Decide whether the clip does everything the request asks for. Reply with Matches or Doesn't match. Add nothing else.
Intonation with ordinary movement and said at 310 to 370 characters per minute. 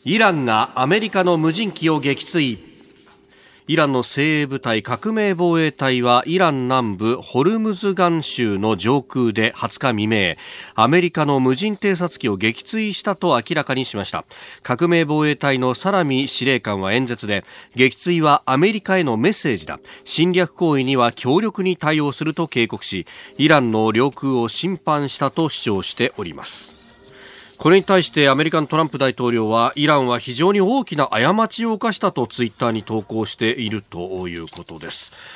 Doesn't match